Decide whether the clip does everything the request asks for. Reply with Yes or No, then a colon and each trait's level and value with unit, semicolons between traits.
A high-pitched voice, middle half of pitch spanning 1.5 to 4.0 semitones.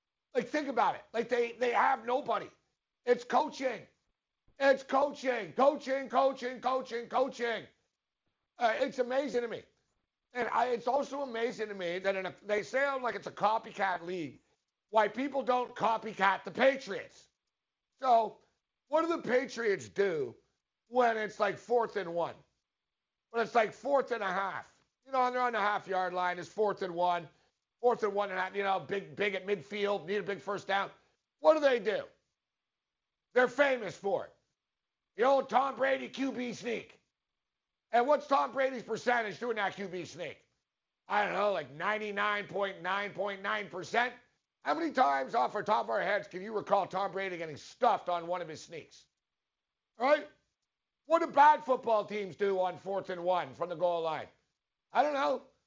No: high, 220 Hz; average, 4.9 semitones